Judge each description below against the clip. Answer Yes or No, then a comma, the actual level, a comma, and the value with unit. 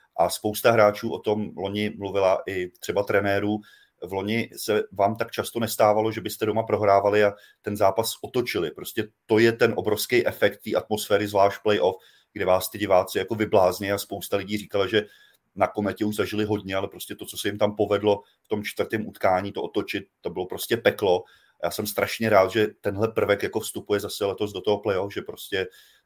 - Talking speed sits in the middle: No, fast, 195 wpm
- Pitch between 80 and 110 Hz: Yes, low, 105 Hz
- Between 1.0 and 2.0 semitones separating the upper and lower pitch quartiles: Yes, narrow, 1.3 semitones